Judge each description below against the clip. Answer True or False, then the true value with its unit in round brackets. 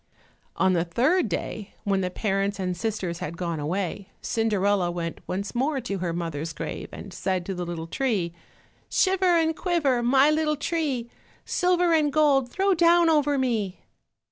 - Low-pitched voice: False (220 Hz)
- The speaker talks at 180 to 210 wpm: False (165 wpm)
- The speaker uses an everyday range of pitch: False (8.8 semitones)